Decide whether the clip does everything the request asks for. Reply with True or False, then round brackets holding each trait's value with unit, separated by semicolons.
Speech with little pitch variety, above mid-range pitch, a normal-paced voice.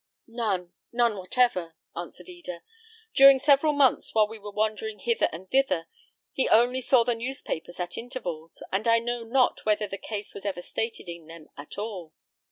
False (5.4 semitones; 220 Hz; 175 wpm)